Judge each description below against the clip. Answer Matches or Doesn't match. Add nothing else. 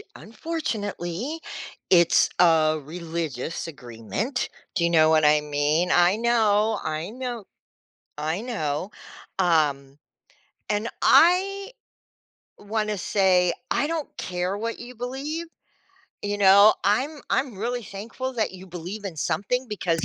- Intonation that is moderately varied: Doesn't match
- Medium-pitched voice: Doesn't match